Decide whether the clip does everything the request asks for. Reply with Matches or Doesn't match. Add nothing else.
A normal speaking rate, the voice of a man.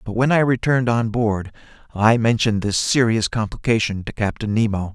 Matches